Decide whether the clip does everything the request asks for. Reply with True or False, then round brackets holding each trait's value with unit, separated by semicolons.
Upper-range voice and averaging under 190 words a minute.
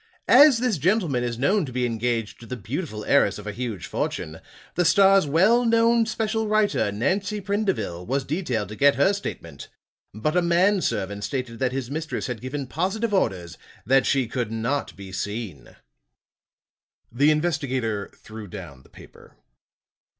False (135 Hz; 160 wpm)